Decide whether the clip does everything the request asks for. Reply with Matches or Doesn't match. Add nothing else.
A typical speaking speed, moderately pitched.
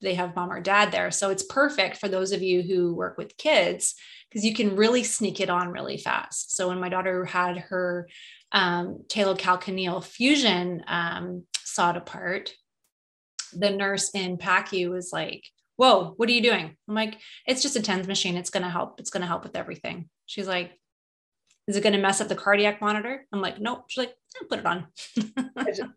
Doesn't match